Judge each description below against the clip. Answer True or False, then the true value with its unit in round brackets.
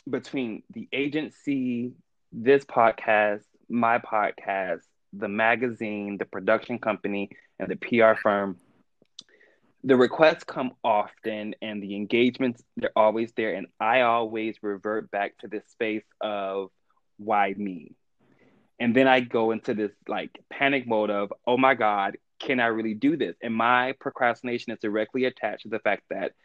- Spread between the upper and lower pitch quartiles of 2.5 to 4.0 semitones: True (3.0 semitones)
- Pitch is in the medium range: False (115 Hz)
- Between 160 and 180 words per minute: False (145 wpm)